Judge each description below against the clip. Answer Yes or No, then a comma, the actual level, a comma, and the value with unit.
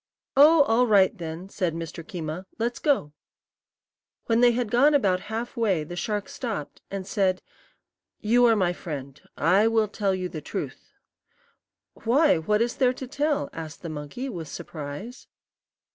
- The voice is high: Yes, high, 205 Hz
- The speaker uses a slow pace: No, average, 160 wpm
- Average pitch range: No, wide, 6.2 semitones